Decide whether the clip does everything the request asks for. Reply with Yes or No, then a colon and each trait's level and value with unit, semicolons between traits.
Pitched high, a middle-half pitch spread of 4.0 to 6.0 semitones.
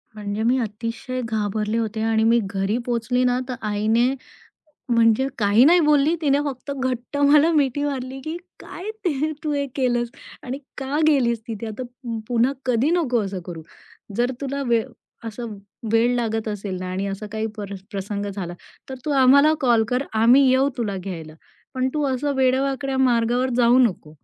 No: high, 240 Hz; average, 3.5 semitones